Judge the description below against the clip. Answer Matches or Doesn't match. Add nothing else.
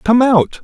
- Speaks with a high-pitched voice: Matches